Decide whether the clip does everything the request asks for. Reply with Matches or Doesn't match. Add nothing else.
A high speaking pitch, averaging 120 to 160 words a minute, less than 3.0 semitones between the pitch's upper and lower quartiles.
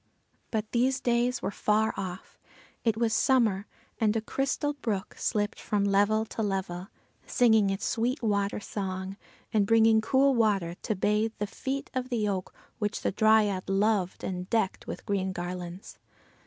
Matches